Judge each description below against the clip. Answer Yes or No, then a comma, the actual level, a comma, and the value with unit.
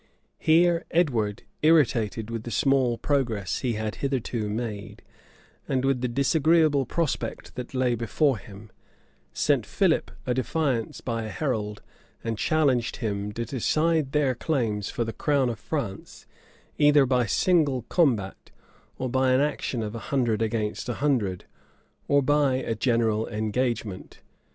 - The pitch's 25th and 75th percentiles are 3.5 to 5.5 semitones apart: Yes, average, 4.2 semitones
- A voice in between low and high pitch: No, low, 125 Hz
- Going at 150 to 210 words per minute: No, average, 140 wpm